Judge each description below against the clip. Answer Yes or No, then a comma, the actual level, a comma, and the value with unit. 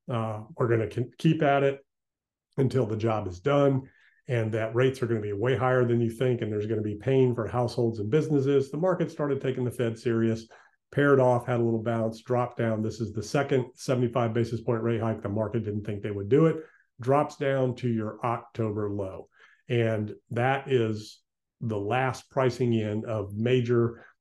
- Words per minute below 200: No, fast, 205 wpm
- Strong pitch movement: No, average, 2.8 semitones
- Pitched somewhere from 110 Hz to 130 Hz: Yes, low, 120 Hz